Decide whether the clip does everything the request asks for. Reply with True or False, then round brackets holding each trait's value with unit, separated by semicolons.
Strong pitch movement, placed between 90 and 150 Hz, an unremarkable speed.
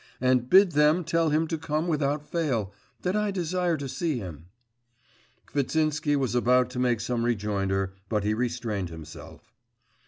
True (6.2 semitones; 135 Hz; 155 wpm)